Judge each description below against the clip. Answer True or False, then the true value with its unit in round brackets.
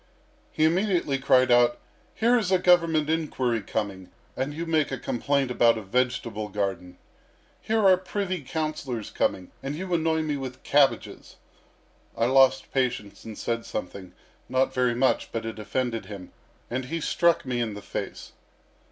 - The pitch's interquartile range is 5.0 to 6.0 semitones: True (5.6 semitones)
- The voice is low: True (130 Hz)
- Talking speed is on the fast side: False (160 wpm)